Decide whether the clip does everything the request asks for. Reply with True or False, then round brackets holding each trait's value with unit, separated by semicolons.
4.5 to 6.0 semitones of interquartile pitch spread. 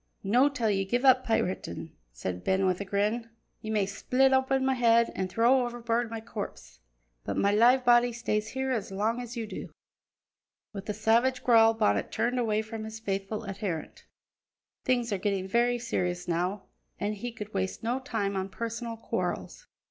False (3.4 semitones)